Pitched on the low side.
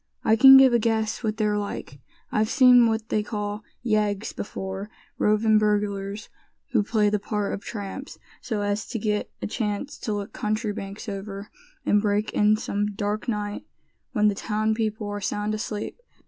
No: high, 210 Hz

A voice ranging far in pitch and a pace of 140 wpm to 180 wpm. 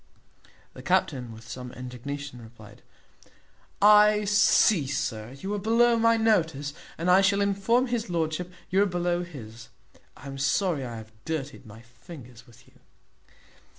Yes: wide, 8.3 semitones; average, 150 wpm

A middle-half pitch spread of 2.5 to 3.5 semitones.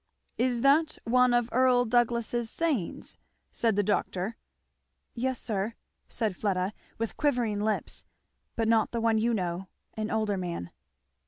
Yes: average, 2.8 semitones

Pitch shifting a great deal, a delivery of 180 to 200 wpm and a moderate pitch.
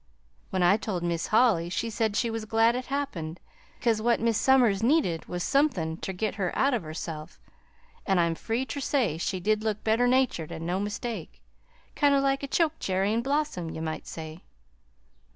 No: wide, 6.1 semitones; average, 190 wpm; high, 215 Hz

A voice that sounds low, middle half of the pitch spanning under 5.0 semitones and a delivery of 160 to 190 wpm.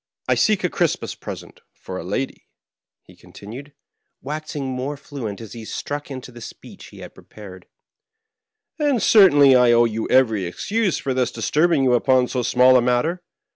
Yes: low, 130 Hz; average, 4.4 semitones; average, 175 wpm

